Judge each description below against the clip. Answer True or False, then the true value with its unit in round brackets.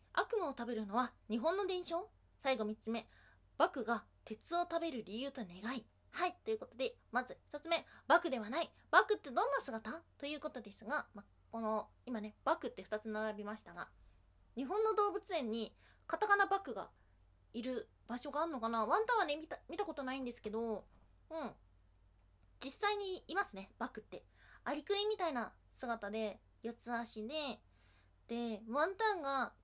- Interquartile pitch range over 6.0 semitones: True (7.5 semitones)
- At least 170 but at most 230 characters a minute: False (320 characters per minute)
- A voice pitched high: True (255 Hz)